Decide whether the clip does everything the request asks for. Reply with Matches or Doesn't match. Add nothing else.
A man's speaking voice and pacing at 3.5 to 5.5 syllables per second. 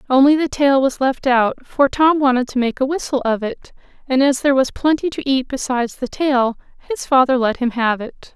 Doesn't match